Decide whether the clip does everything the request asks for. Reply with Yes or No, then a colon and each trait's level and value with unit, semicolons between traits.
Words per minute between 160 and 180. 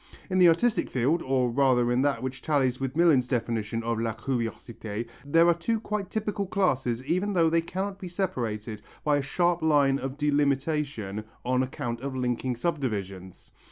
Yes: average, 170 wpm